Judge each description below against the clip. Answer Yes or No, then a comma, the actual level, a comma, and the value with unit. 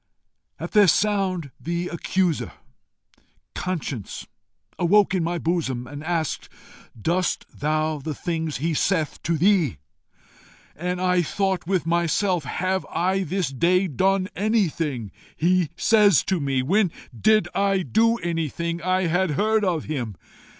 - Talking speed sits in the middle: No, slow, 130 wpm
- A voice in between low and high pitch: Yes, medium, 175 Hz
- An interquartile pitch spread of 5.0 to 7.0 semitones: No, average, 3.3 semitones